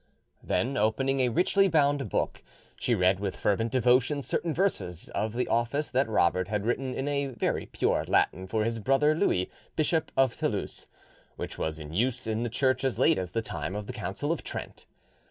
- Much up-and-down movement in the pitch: No, average, 4.8 semitones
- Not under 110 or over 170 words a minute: No, average, 190 wpm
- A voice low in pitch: Yes, low, 120 Hz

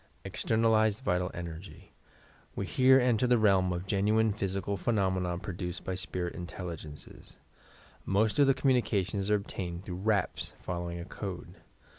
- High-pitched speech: No, very low, 95 Hz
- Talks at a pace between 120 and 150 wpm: Yes, average, 140 wpm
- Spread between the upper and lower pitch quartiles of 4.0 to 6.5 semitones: No, average, 3.5 semitones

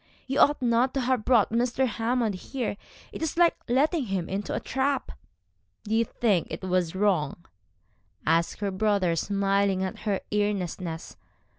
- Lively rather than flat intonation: No, average, 4.9 semitones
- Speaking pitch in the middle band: No, high, 210 Hz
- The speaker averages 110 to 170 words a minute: Yes, average, 155 wpm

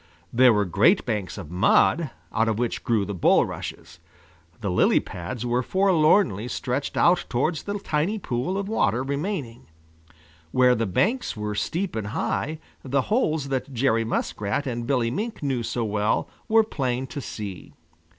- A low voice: Yes, low, 125 Hz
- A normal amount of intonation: No, wide, 6.1 semitones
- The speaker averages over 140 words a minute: Yes, average, 160 wpm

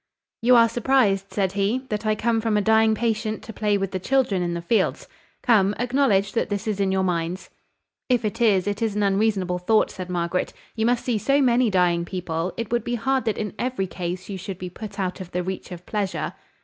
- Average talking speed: No, fast, 230 wpm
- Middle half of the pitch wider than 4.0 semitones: No, average, 3.6 semitones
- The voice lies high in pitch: Yes, high, 205 Hz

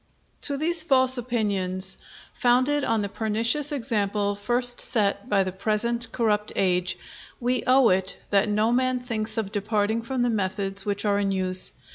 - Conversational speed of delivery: Yes, average, 160 wpm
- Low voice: No, high, 215 Hz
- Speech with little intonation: No, average, 3.5 semitones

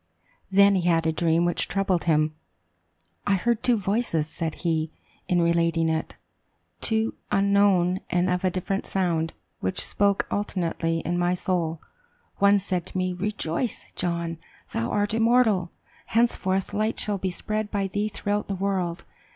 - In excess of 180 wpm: No, average, 150 wpm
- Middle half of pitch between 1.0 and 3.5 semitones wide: Yes, average, 3.2 semitones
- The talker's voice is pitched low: No, medium, 185 Hz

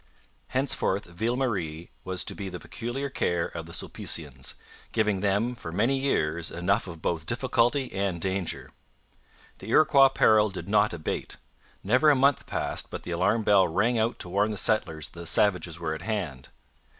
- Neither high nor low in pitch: No, low, 100 Hz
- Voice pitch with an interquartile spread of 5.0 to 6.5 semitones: Yes, wide, 5.4 semitones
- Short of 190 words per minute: Yes, average, 175 wpm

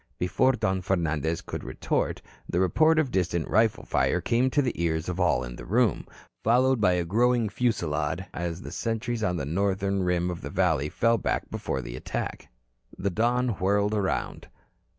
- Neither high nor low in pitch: No, very low, 95 Hz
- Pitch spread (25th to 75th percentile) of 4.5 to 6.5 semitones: Yes, average, 5.2 semitones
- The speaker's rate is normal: Yes, average, 170 wpm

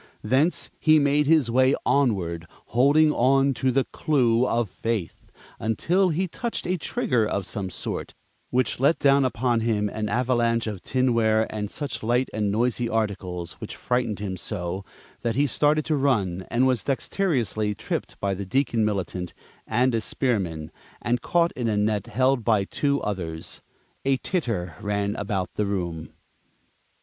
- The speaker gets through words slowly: No, average, 155 wpm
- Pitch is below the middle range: Yes, low, 115 Hz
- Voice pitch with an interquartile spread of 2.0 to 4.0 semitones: No, average, 4.6 semitones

